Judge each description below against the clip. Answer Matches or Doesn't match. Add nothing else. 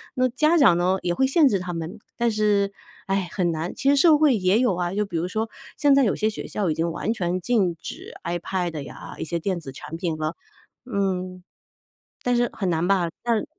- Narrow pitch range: Doesn't match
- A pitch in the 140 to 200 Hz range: Matches